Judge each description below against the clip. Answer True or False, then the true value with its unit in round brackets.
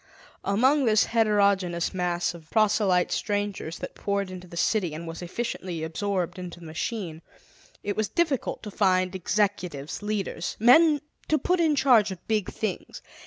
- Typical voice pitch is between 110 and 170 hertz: False (200 Hz)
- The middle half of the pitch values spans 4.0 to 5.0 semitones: False (3.6 semitones)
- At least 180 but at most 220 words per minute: False (160 wpm)